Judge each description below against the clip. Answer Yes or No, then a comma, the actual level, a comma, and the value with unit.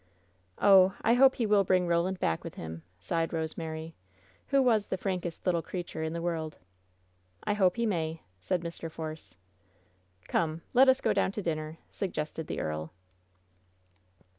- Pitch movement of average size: Yes, average, 3.5 semitones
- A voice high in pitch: No, medium, 170 Hz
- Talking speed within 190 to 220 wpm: No, average, 160 wpm